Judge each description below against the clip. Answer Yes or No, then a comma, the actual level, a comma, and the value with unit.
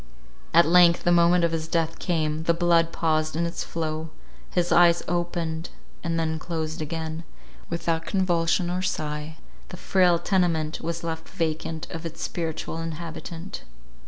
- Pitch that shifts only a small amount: Yes, narrow, 1.3 semitones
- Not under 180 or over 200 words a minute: No, average, 150 wpm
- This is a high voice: No, medium, 165 Hz